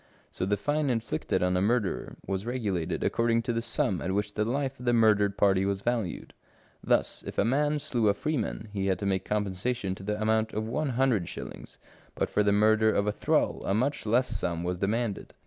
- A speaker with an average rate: No, fast, 215 wpm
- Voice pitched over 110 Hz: No, low, 105 Hz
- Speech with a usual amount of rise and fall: Yes, average, 3.6 semitones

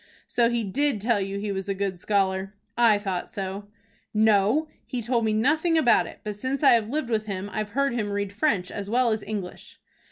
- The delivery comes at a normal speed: No, fast, 215 wpm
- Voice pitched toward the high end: Yes, high, 215 Hz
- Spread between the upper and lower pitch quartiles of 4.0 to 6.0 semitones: No, average, 3.2 semitones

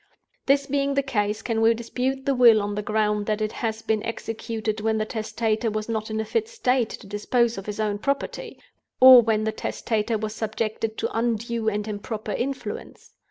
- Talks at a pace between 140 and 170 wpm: No, average, 195 wpm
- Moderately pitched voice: No, high, 220 Hz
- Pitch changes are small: Yes, narrow, 2.0 semitones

